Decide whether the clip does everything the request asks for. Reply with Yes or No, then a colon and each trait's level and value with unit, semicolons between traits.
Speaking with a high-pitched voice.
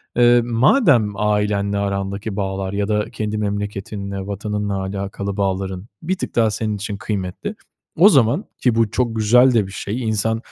No: low, 105 Hz